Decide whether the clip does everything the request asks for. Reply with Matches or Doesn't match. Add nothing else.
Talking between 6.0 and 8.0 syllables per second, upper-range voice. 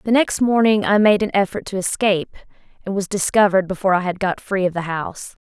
Matches